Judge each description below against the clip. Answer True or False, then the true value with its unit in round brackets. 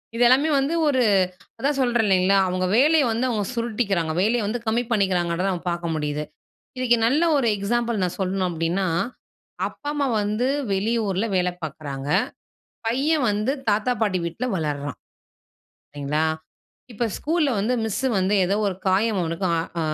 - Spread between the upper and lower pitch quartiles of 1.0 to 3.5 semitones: False (5.2 semitones)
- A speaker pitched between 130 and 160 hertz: False (205 Hz)